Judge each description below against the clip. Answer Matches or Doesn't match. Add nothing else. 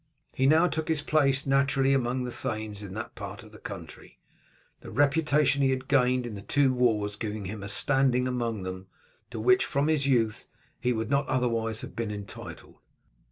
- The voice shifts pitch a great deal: Doesn't match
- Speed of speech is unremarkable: Matches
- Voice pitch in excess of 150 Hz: Doesn't match